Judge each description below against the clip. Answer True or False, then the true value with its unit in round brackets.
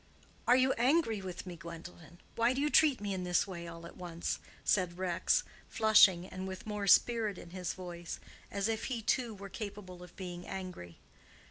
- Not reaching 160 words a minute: False (190 wpm)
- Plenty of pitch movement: False (3.8 semitones)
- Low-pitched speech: False (190 Hz)